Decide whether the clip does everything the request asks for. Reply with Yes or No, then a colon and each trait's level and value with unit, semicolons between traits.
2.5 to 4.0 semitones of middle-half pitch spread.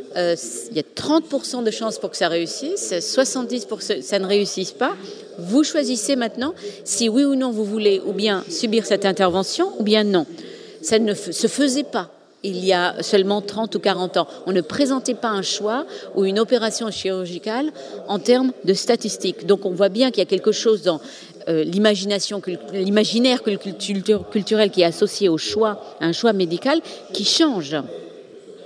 No: average, 4.7 semitones